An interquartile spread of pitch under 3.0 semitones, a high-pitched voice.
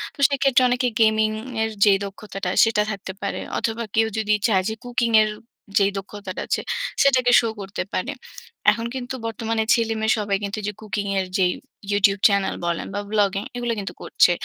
Yes: narrow, 2.4 semitones; high, 215 Hz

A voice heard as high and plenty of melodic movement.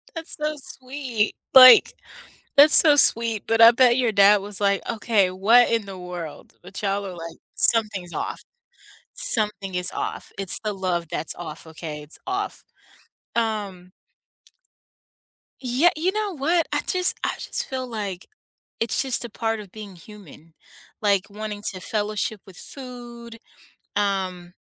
No: high, 210 Hz; average, 4.4 semitones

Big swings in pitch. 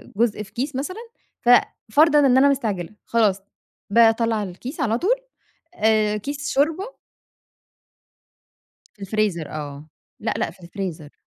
Yes: wide, 6.1 semitones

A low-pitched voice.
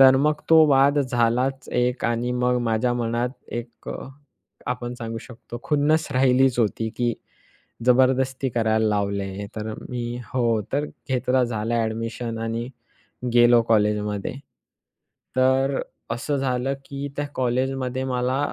Yes: low, 125 Hz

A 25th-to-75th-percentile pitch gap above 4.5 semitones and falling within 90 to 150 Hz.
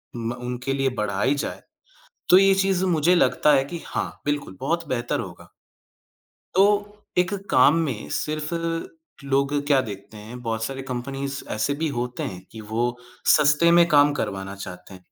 Yes: average, 5.2 semitones; low, 135 Hz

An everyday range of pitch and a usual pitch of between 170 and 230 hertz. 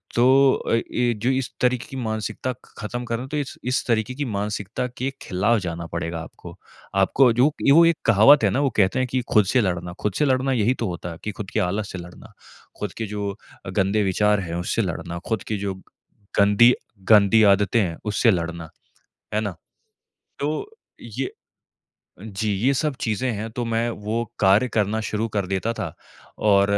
No: average, 4.1 semitones; low, 110 Hz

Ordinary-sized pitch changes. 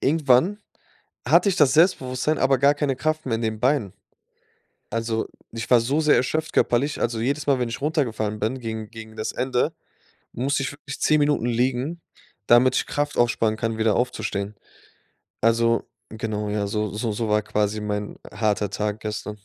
Yes: average, 4.4 semitones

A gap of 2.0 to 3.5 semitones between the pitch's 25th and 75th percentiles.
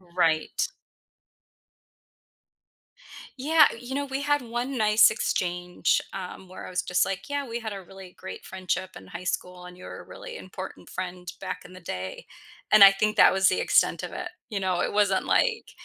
No: average, 4.9 semitones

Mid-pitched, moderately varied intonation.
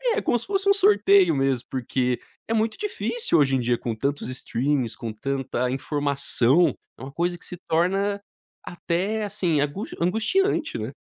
No: medium, 165 Hz; wide, 8.4 semitones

